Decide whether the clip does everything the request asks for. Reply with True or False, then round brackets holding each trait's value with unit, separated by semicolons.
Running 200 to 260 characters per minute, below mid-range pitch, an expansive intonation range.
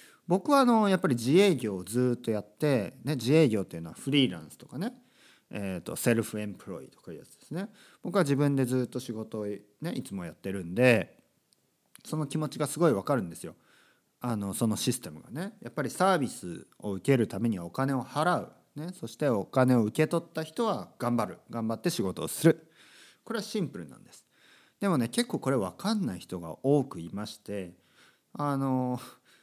False (375 characters per minute; 130 Hz; 6.7 semitones)